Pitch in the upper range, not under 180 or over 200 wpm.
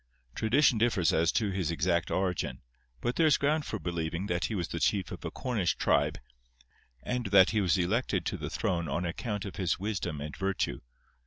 No: very low, 95 Hz; average, 195 wpm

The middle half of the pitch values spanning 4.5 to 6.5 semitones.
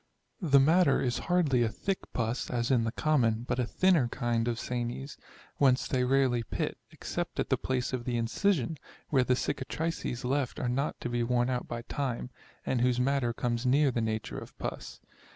No: narrow, 2.6 semitones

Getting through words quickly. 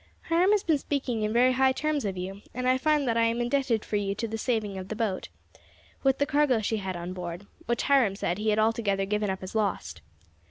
Yes: fast, 240 wpm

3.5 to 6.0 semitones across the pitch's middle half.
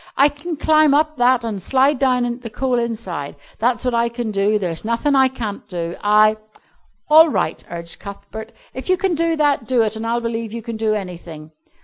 Yes: average, 4.1 semitones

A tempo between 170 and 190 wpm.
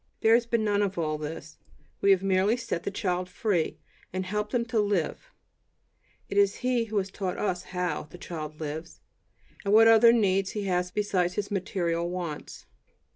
Yes: average, 180 wpm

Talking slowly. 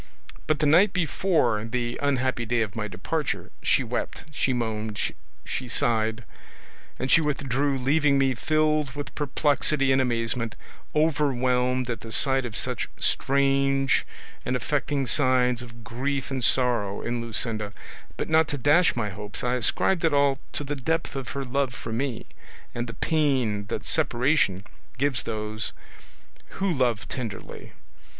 No: average, 150 wpm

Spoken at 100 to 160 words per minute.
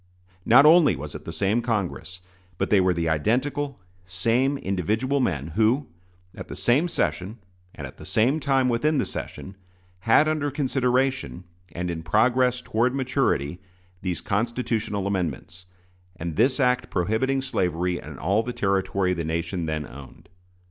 Yes: average, 150 wpm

